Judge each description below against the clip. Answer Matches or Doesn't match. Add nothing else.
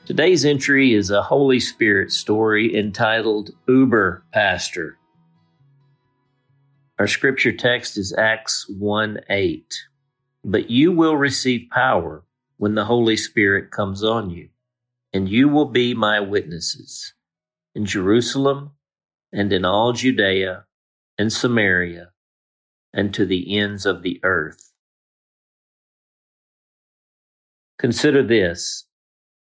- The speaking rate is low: Matches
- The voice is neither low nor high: Doesn't match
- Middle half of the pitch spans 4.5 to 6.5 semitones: Matches